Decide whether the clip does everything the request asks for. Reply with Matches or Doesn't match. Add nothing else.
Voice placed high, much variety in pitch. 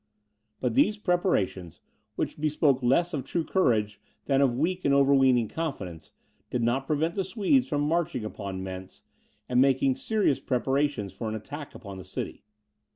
Doesn't match